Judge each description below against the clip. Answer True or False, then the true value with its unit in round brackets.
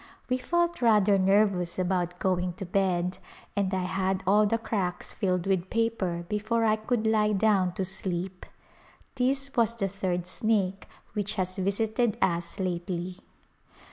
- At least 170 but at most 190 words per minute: False (145 wpm)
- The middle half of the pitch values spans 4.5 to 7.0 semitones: False (3.1 semitones)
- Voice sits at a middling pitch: False (195 Hz)